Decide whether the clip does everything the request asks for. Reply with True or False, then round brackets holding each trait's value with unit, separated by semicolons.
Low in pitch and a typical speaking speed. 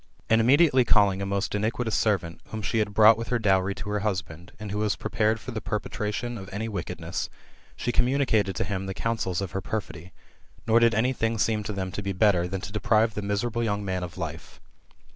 False (105 Hz; 220 wpm)